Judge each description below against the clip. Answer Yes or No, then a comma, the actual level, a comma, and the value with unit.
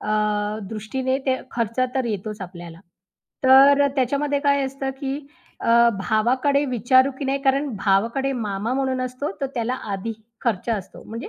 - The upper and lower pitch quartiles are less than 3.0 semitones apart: No, average, 3.8 semitones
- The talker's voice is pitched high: Yes, very high, 255 Hz